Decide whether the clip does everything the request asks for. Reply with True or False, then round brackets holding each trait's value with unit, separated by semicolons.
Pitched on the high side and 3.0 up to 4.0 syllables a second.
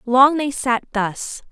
True (250 Hz; 3.3 syllables/s)